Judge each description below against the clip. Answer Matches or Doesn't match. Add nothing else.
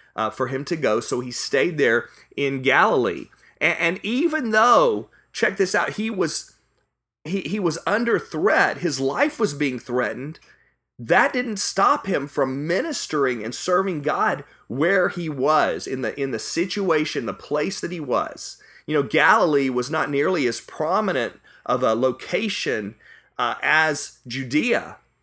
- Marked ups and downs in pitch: Matches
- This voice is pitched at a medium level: Matches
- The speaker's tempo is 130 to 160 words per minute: Matches